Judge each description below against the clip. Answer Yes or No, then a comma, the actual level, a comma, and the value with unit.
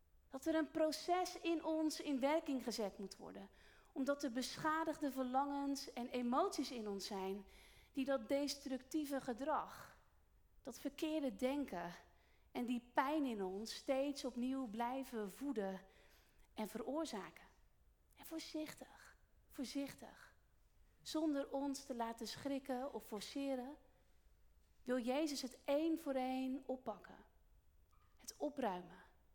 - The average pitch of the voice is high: Yes, very high, 270 Hz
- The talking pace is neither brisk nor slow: No, slow, 115 wpm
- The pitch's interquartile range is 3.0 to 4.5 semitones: Yes, average, 3.4 semitones